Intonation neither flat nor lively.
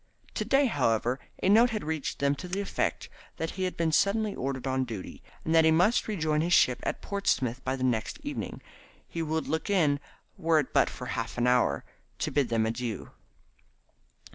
No: wide, 6.3 semitones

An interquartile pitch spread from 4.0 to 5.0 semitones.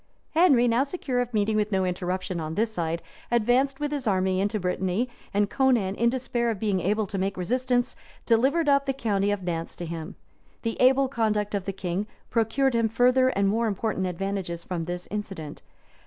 Yes: average, 4.7 semitones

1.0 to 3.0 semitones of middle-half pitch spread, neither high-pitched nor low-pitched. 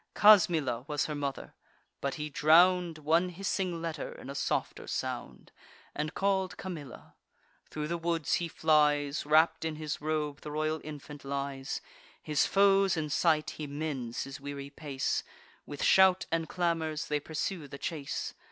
Yes: average, 2.7 semitones; medium, 155 Hz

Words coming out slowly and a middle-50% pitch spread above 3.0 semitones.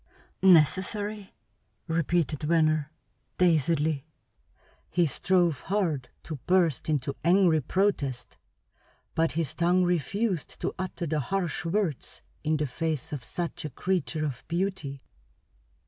Yes: slow, 115 wpm; average, 3.4 semitones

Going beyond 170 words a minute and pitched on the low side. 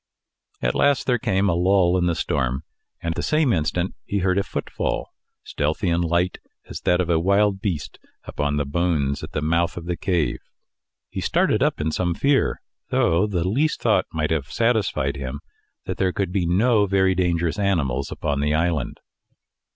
Yes: average, 180 wpm; very low, 85 Hz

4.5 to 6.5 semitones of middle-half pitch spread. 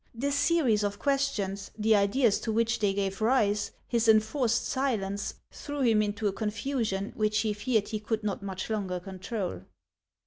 No: average, 2.8 semitones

